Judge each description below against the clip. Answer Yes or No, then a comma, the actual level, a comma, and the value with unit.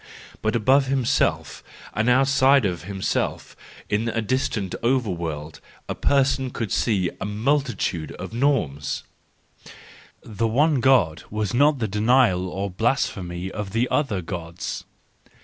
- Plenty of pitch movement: Yes, wide, 6.0 semitones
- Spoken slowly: Yes, slow, 130 wpm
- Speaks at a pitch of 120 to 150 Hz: No, low, 110 Hz